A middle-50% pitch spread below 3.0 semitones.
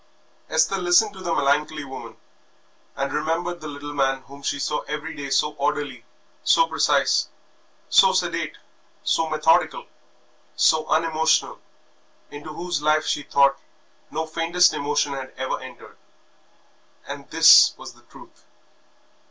Yes: narrow, 2.5 semitones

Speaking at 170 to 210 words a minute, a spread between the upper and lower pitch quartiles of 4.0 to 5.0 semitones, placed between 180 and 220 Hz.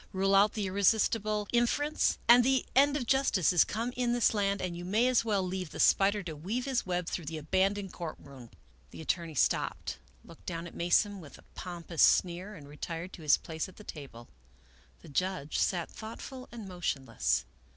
Yes: average, 195 wpm; average, 4.6 semitones; high, 190 Hz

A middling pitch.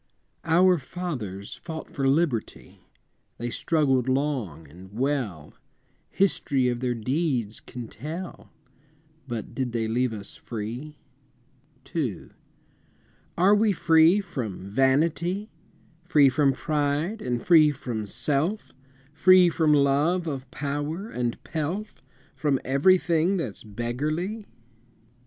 Yes: medium, 145 Hz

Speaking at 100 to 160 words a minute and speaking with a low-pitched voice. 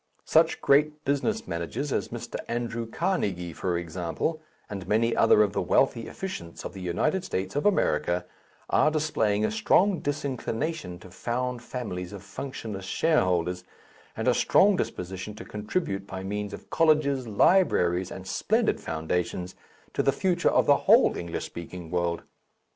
Yes: average, 150 wpm; low, 105 Hz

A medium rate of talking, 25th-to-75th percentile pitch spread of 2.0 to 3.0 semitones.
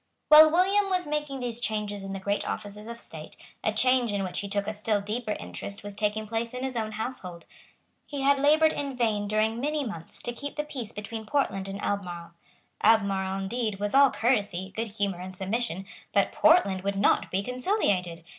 No: average, 195 wpm; average, 4.5 semitones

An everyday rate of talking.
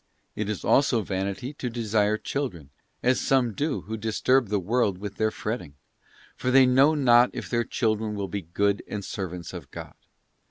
Yes: average, 175 wpm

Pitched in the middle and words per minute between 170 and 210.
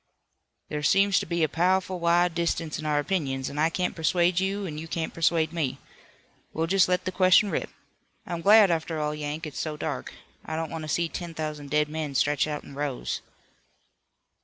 Yes: medium, 165 Hz; average, 200 wpm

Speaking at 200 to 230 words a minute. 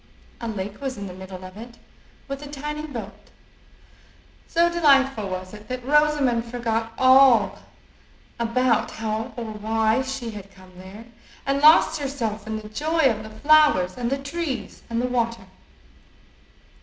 No: average, 155 wpm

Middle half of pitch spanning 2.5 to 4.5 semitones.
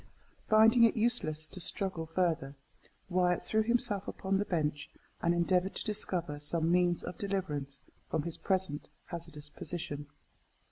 Yes: average, 3.8 semitones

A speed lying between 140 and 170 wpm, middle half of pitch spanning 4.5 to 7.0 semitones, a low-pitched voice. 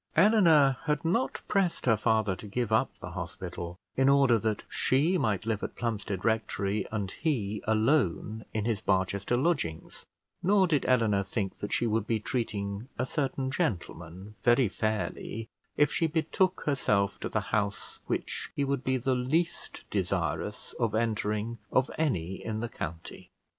Yes: average, 160 wpm; average, 5.0 semitones; low, 115 Hz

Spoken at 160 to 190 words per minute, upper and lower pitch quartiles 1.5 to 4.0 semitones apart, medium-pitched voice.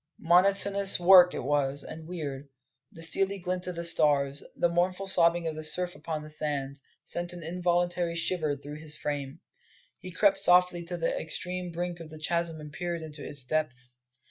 Yes: average, 180 wpm; average, 3.0 semitones; medium, 170 Hz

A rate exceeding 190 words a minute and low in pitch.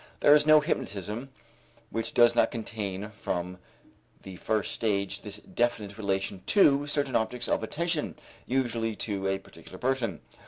No: average, 145 wpm; low, 110 Hz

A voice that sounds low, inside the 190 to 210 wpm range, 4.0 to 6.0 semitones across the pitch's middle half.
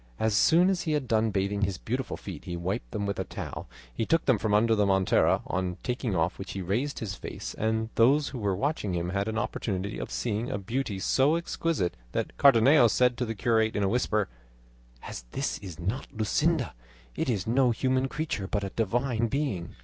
Yes: low, 110 Hz; fast, 205 wpm; average, 4.8 semitones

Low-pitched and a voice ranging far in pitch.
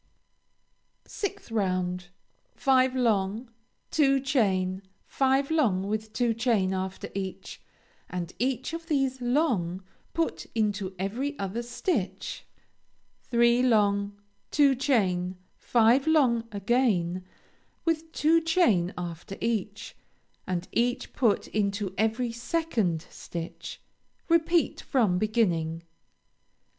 No: high, 225 Hz; wide, 5.8 semitones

